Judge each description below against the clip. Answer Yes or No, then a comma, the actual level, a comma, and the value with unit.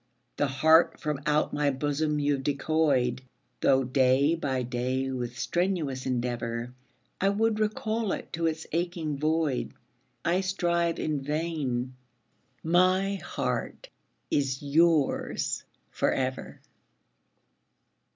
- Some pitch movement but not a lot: Yes, average, 4.3 semitones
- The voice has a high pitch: No, medium, 150 Hz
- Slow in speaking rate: Yes, slow, 110 wpm